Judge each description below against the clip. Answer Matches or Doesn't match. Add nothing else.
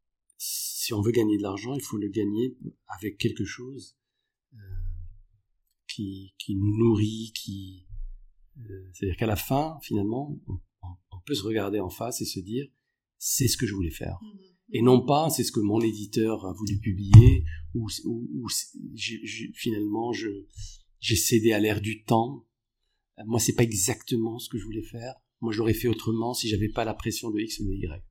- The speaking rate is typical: Matches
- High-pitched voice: Doesn't match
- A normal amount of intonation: Matches